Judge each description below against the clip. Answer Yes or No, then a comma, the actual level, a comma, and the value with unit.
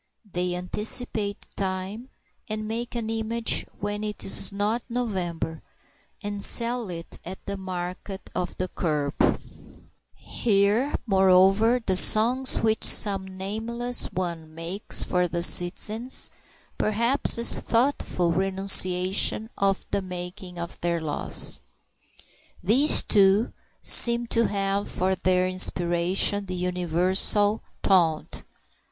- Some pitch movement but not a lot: Yes, average, 3.4 semitones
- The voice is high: Yes, high, 195 Hz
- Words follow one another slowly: Yes, slow, 110 wpm